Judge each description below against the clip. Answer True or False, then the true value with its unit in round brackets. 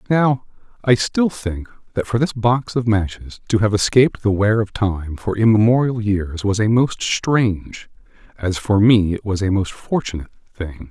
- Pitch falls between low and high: False (110 Hz)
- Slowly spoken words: False (180 wpm)